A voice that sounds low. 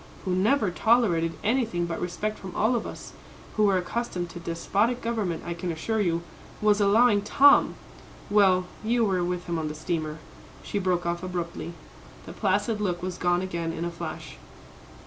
No: medium, 185 Hz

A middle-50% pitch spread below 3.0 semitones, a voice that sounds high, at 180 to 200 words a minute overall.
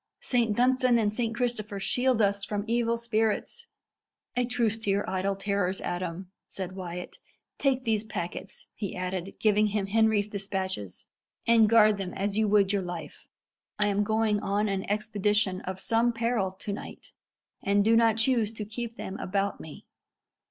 No: narrow, 2.6 semitones; high, 210 Hz; average, 165 wpm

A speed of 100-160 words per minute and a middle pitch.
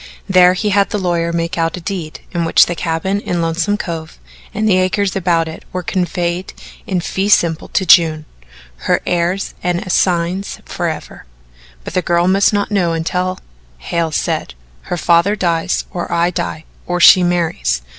No: average, 170 wpm; medium, 175 Hz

